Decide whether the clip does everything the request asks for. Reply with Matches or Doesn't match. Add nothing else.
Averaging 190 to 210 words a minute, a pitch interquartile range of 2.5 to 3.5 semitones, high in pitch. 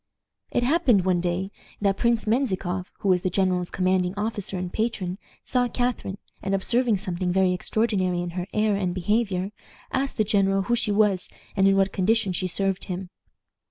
Doesn't match